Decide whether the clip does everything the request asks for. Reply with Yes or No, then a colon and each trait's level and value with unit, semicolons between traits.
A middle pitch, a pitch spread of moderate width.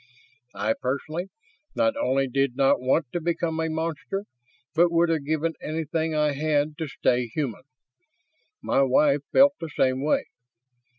Yes: medium, 155 Hz; average, 3.2 semitones